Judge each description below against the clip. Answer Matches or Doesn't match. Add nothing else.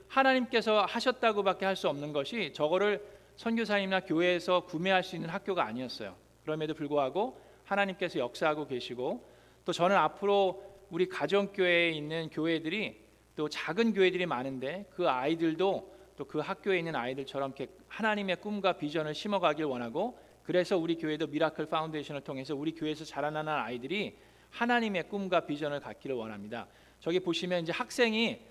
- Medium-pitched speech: Matches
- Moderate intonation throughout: Matches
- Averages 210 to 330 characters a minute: Doesn't match